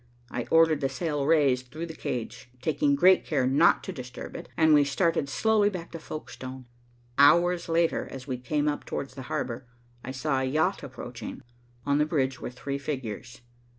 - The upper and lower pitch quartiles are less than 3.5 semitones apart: No, average, 3.9 semitones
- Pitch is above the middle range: No, medium, 140 Hz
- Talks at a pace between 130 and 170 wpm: No, average, 185 wpm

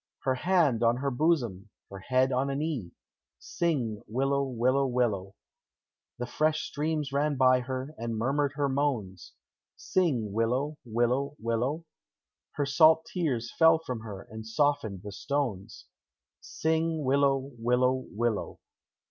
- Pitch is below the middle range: Yes, low, 130 Hz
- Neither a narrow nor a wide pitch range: Yes, average, 4.0 semitones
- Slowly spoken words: Yes, slow, 130 wpm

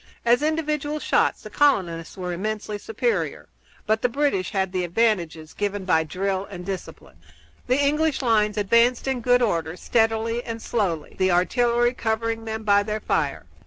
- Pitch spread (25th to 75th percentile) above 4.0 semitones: Yes, average, 4.5 semitones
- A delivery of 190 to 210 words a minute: No, average, 160 wpm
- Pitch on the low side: No, high, 220 Hz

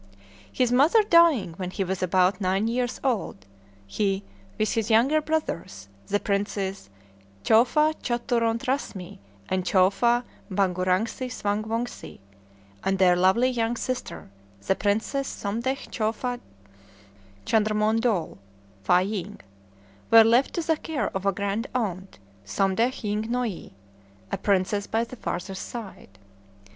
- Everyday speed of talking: No, slow, 125 wpm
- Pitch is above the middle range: Yes, high, 215 Hz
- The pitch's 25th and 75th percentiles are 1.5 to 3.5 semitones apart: No, average, 4.1 semitones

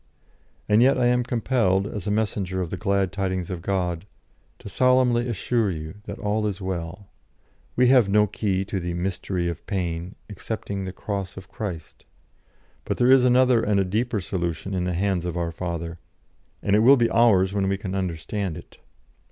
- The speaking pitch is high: No, low, 100 Hz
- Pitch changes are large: No, average, 3.3 semitones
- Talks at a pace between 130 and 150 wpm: No, average, 185 wpm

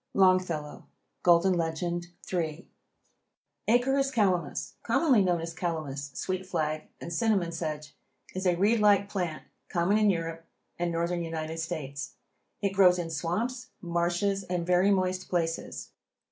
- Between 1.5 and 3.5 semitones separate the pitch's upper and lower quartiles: Yes, average, 2.8 semitones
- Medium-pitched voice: Yes, medium, 175 Hz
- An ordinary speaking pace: No, slow, 130 wpm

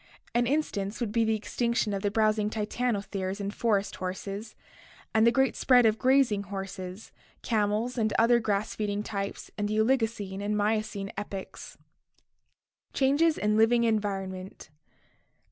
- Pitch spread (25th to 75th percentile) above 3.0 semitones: No, average, 2.7 semitones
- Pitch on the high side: Yes, high, 215 Hz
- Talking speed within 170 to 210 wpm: No, average, 140 wpm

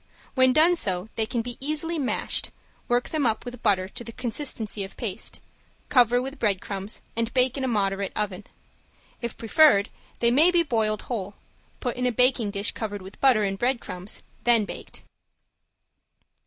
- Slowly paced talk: No, average, 170 wpm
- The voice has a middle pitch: No, high, 235 Hz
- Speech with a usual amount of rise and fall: Yes, average, 4.0 semitones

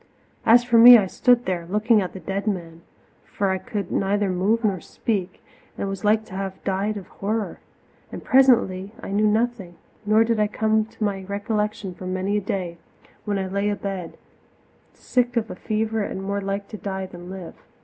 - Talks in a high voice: Yes, high, 200 Hz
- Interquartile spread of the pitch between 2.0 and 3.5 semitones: Yes, narrow, 2.4 semitones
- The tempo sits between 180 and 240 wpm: Yes, average, 190 wpm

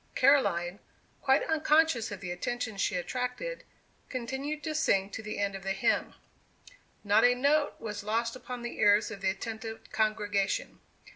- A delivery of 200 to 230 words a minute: No, average, 155 wpm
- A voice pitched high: Yes, high, 225 Hz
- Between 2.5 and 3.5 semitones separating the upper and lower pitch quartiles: No, average, 4.4 semitones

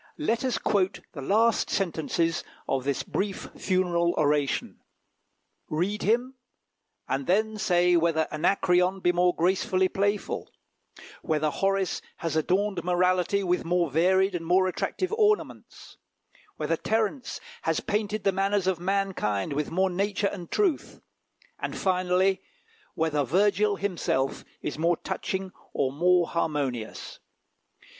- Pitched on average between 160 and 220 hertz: Yes, medium, 185 Hz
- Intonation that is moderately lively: Yes, average, 3.3 semitones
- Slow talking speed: Yes, slow, 125 wpm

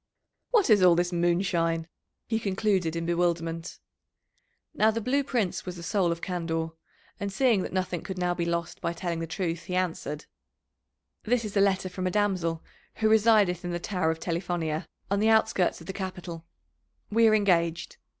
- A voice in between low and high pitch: Yes, medium, 180 Hz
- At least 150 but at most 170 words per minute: No, average, 180 wpm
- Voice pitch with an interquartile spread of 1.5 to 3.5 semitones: Yes, average, 3.2 semitones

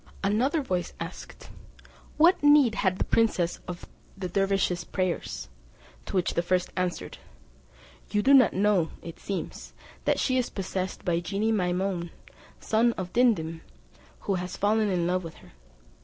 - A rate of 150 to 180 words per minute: Yes, average, 155 wpm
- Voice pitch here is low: No, high, 190 Hz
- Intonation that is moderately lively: Yes, average, 3.7 semitones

